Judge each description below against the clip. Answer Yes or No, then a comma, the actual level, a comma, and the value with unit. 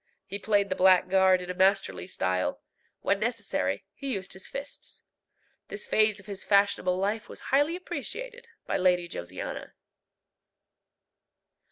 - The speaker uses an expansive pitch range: No, average, 2.9 semitones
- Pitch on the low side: No, high, 190 Hz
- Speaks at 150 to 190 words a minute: No, slow, 135 wpm